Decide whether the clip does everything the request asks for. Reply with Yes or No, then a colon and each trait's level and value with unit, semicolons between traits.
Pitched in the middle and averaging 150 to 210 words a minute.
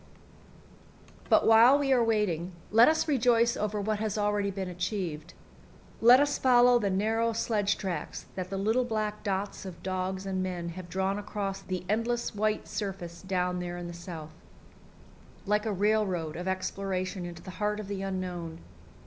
No: high, 195 Hz; average, 165 wpm